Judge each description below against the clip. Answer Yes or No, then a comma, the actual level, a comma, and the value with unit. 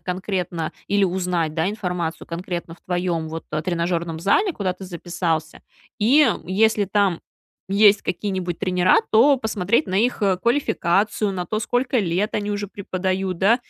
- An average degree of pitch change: Yes, average, 3.2 semitones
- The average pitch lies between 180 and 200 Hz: Yes, medium, 185 Hz